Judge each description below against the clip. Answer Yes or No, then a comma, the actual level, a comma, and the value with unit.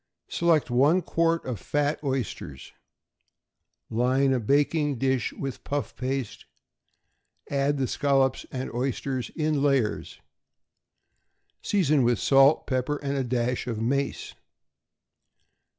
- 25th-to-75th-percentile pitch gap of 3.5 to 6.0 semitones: No, narrow, 2.4 semitones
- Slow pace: Yes, slow, 110 wpm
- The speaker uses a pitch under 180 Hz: Yes, low, 135 Hz